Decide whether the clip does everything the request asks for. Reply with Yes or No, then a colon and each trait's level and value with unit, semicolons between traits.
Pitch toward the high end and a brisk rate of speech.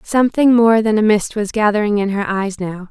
Yes: high, 210 Hz; fast, 225 wpm